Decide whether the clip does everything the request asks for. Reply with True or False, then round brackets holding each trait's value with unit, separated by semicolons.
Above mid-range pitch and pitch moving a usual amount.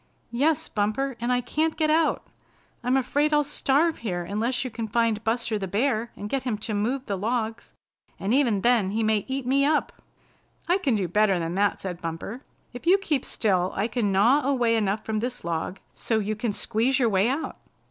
True (230 Hz; 4.5 semitones)